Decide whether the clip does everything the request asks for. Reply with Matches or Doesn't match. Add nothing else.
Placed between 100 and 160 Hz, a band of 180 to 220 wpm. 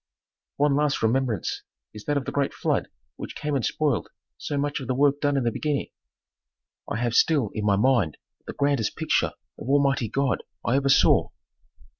Matches